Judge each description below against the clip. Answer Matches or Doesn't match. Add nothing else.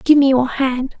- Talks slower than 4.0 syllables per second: Doesn't match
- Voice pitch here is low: Doesn't match